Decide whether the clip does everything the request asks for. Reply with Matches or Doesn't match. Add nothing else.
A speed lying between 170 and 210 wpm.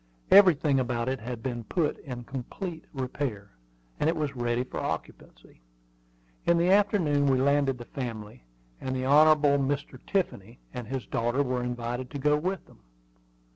Doesn't match